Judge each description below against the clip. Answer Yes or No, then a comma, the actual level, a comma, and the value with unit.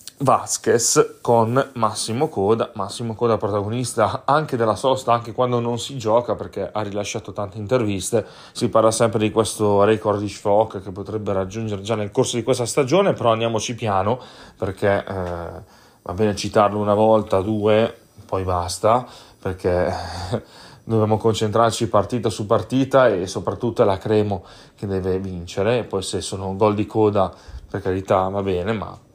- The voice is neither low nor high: No, low, 110 Hz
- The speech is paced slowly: No, average, 155 wpm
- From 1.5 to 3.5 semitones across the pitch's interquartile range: Yes, average, 2.8 semitones